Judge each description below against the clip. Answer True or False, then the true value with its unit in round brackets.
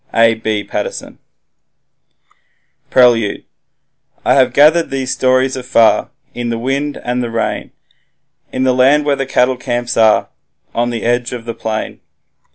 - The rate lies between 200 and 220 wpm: False (145 wpm)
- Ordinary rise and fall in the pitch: False (2.3 semitones)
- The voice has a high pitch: False (125 Hz)